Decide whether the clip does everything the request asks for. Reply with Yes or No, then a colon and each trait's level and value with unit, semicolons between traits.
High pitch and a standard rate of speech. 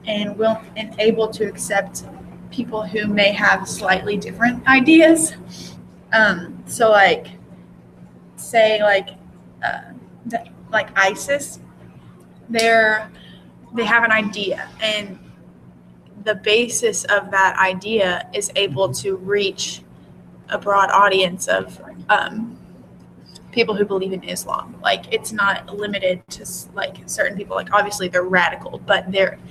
No: high, 195 Hz; slow, 125 wpm